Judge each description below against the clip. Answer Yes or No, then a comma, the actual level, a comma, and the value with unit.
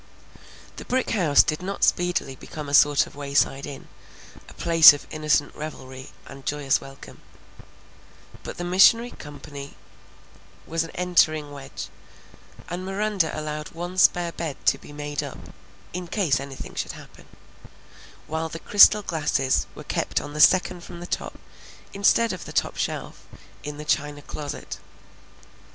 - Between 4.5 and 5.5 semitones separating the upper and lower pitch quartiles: No, average, 3.5 semitones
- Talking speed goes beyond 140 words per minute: Yes, average, 150 wpm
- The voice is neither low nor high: Yes, medium, 155 Hz